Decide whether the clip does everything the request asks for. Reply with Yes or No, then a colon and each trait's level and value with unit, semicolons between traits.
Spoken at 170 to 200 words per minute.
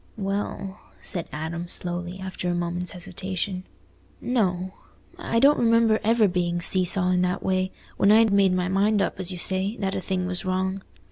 Yes: average, 180 wpm